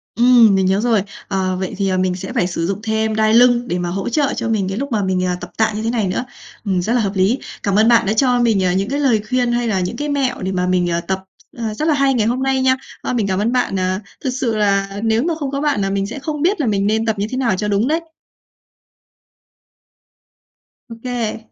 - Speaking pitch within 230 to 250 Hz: No, high, 220 Hz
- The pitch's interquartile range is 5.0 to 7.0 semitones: No, average, 4.4 semitones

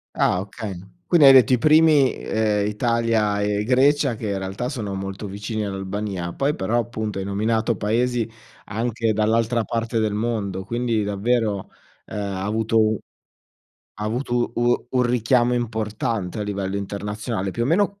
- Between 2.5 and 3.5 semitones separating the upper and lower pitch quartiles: Yes, average, 2.8 semitones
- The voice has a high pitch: No, low, 110 Hz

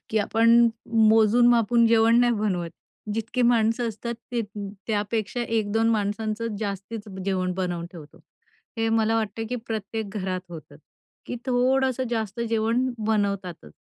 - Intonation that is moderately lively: No, narrow, 2.2 semitones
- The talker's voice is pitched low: No, high, 220 Hz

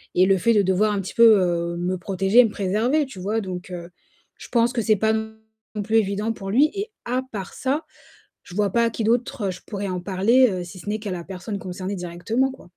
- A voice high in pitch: Yes, high, 205 Hz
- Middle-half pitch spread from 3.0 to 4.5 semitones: Yes, average, 3.6 semitones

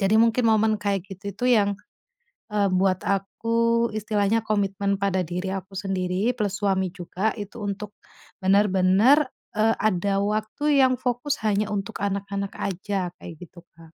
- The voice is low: No, high, 200 Hz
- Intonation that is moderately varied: No, narrow, 2.1 semitones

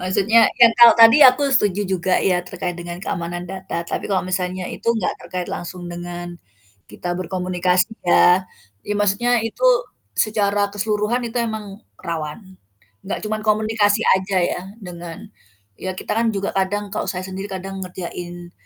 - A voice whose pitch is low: No, high, 190 Hz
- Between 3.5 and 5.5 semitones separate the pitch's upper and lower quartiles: No, average, 2.7 semitones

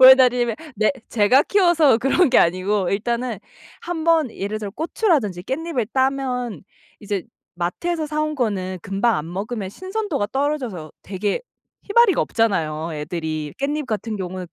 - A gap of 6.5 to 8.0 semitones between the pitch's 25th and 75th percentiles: Yes, wide, 7.3 semitones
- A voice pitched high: Yes, high, 235 Hz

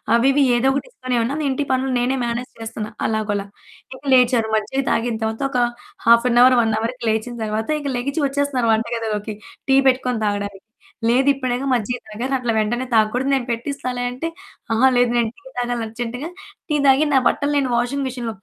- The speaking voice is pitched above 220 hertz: Yes, high, 245 Hz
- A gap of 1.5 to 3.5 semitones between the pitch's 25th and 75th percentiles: Yes, average, 2.8 semitones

